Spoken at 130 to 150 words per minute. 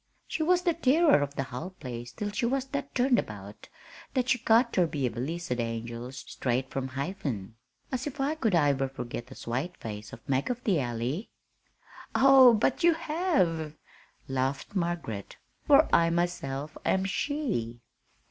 No: average, 165 wpm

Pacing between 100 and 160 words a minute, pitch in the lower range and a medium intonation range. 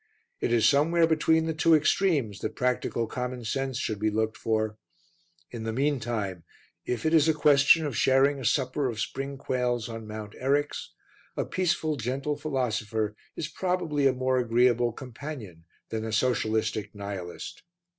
Yes: average, 155 wpm; low, 125 Hz; average, 4.7 semitones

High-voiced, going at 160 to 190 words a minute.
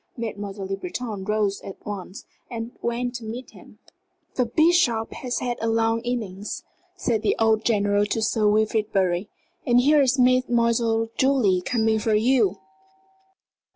No: high, 225 Hz; average, 150 wpm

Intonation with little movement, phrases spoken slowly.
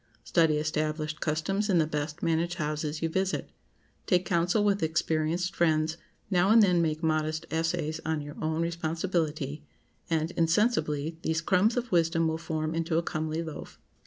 No: narrow, 1.9 semitones; average, 160 wpm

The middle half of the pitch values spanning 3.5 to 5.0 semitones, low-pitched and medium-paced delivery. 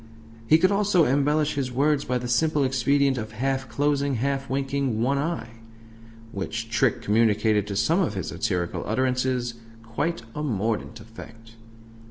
Yes: average, 3.9 semitones; low, 130 Hz; average, 150 wpm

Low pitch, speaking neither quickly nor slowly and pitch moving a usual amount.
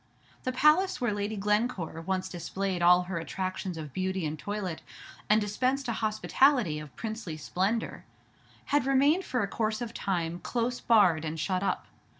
No: high, 200 Hz; average, 160 wpm; average, 5.0 semitones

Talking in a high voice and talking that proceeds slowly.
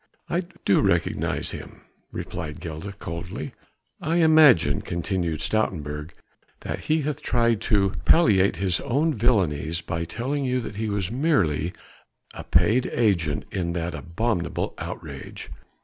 No: low, 100 Hz; slow, 130 wpm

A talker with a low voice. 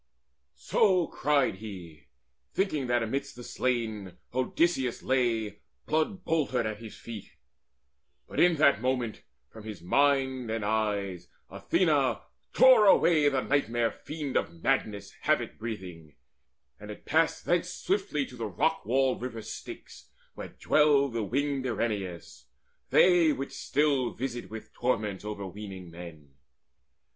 Yes: low, 120 Hz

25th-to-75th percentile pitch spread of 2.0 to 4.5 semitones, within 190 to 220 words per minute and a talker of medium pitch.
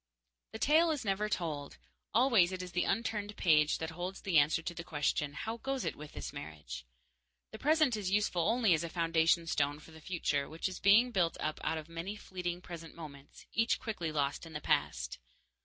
No: average, 5.3 semitones; fast, 205 wpm; medium, 175 Hz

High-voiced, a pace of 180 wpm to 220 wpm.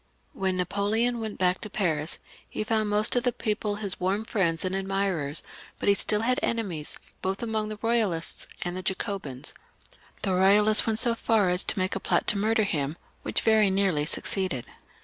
Yes: high, 200 Hz; average, 185 wpm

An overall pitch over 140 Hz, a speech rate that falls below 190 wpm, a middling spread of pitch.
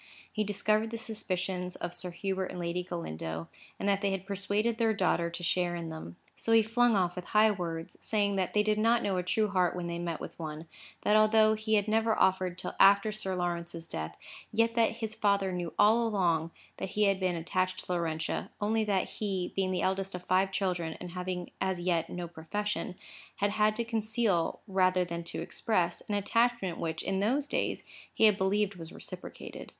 No: high, 190 Hz; fast, 205 wpm; average, 3.3 semitones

